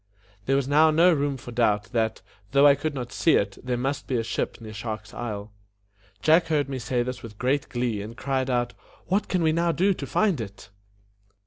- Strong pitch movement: No, average, 4.4 semitones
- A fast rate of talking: Yes, fast, 215 wpm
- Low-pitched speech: Yes, low, 130 Hz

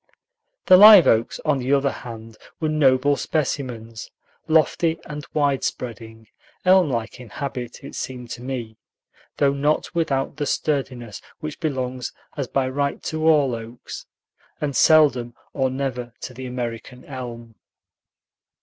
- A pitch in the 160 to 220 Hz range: No, low, 130 Hz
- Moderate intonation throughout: Yes, average, 3.5 semitones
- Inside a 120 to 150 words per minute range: Yes, average, 140 wpm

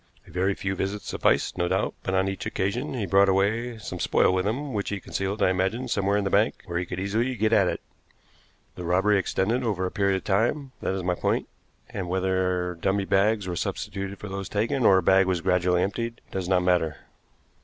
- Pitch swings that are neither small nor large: No, narrow, 2.2 semitones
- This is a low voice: Yes, very low, 95 Hz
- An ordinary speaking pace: No, fast, 220 wpm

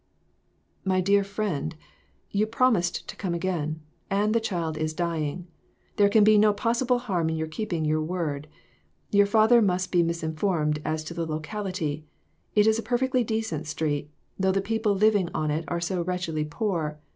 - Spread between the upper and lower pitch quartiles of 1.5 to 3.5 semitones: No, average, 4.9 semitones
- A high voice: No, medium, 180 Hz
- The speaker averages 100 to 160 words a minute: No, average, 175 wpm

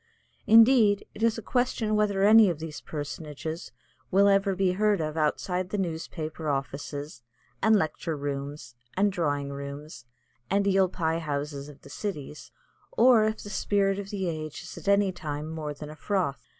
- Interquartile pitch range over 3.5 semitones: Yes, average, 5.2 semitones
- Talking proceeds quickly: No, average, 170 wpm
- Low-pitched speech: No, medium, 170 Hz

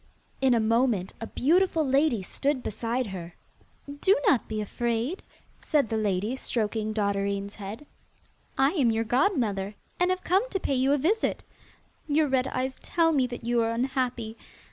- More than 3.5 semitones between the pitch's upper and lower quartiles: Yes, average, 4.7 semitones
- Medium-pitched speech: No, high, 245 Hz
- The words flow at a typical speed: Yes, average, 165 wpm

